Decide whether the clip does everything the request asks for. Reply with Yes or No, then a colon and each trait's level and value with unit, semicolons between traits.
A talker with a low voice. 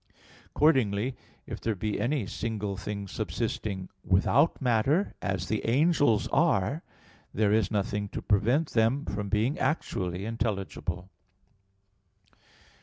Yes: low, 110 Hz